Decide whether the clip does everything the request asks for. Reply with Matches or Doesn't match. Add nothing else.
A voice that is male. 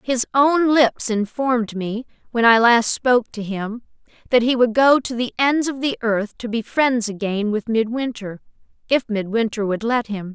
Doesn't match